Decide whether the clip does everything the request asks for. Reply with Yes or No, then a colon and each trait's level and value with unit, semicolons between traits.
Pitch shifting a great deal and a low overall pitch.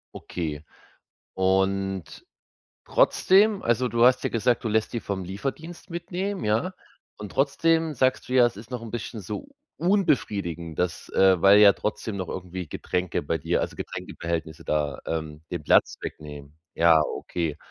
Yes: wide, 7.0 semitones; low, 100 Hz